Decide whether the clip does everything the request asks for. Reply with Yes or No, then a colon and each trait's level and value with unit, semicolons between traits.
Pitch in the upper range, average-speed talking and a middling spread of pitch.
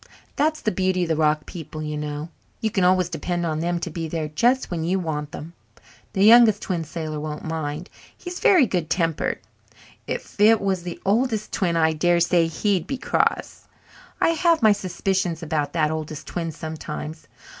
No: medium, 170 Hz; average, 185 wpm; average, 3.9 semitones